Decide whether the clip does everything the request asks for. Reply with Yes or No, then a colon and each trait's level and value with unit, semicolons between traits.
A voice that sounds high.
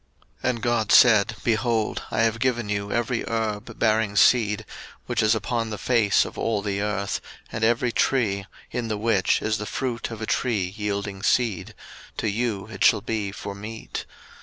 No: low, 110 Hz